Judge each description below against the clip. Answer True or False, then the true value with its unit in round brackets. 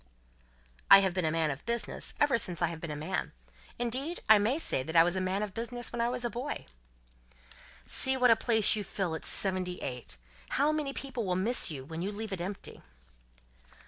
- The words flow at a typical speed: False (210 wpm)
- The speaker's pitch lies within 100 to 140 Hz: False (205 Hz)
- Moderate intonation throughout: False (5.9 semitones)